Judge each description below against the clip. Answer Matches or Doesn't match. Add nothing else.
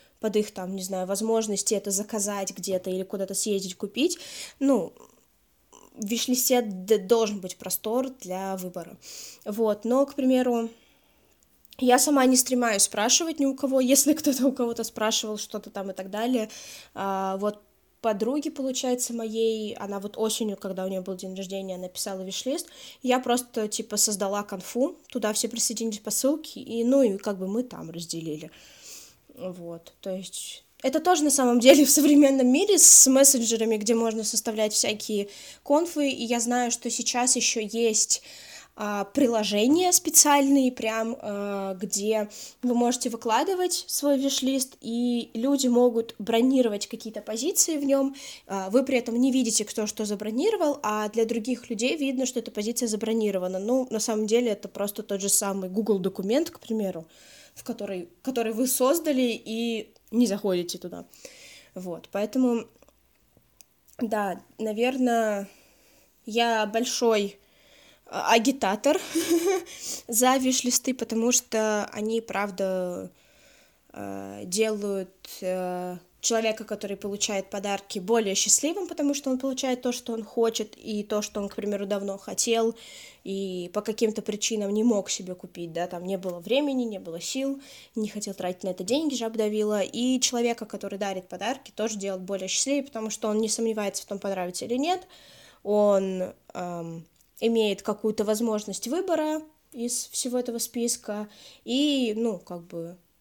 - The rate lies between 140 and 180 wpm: Matches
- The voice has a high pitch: Matches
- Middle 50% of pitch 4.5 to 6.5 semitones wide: Doesn't match